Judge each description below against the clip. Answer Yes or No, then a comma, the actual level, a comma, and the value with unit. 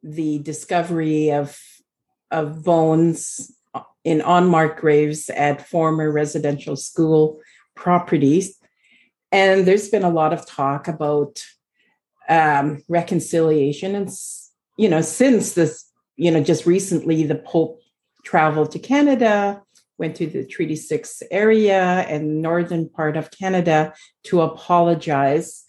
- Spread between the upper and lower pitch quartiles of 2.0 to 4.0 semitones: Yes, narrow, 2.5 semitones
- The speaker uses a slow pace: Yes, slow, 115 wpm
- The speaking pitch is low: No, medium, 160 Hz